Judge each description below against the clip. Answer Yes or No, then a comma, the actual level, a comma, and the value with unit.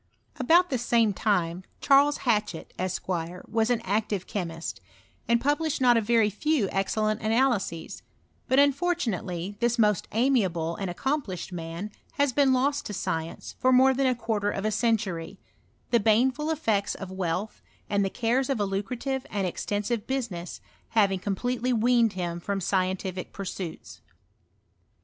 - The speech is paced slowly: No, average, 145 wpm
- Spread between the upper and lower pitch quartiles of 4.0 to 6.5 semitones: Yes, average, 5.1 semitones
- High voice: Yes, high, 215 Hz